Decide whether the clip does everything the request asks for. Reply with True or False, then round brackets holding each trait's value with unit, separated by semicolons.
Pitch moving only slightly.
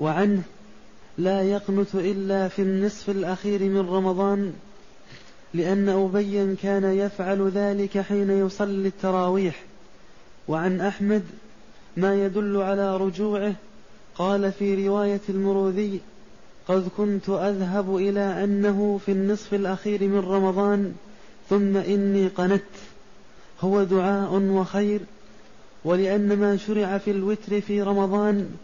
True (1.0 semitones)